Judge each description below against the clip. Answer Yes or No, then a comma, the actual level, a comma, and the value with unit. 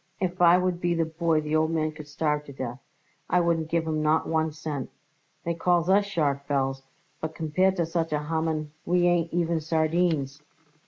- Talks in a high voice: No, medium, 160 Hz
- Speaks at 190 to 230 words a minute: Yes, average, 195 wpm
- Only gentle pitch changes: Yes, narrow, 2.1 semitones